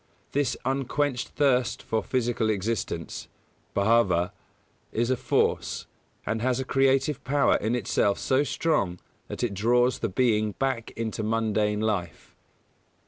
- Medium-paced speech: No, slow, 130 wpm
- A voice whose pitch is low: Yes, low, 115 Hz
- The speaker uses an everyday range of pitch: Yes, average, 3.6 semitones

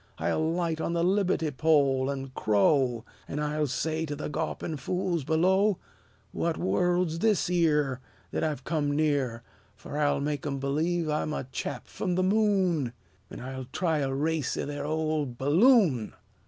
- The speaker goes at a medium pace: Yes, average, 165 wpm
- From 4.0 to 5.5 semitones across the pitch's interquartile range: No, average, 3.6 semitones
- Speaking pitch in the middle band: Yes, medium, 155 Hz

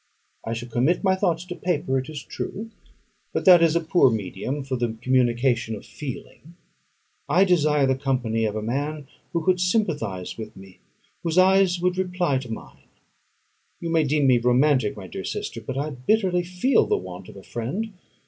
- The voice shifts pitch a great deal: Yes, wide, 6.9 semitones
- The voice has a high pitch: No, medium, 140 Hz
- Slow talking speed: No, average, 185 wpm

